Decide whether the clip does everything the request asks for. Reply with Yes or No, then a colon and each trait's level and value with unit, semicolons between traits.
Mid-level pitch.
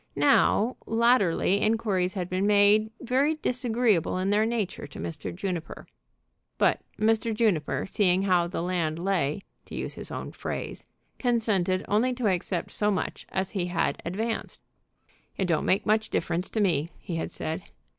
No: high, 195 Hz